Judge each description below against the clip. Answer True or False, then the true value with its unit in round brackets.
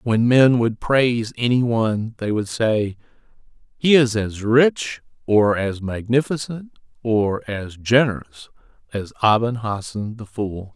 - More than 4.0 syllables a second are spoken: False (3.9 syllables/s)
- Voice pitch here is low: True (115 Hz)